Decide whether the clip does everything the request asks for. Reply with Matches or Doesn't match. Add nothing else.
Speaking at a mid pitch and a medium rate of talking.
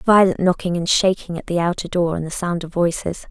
Doesn't match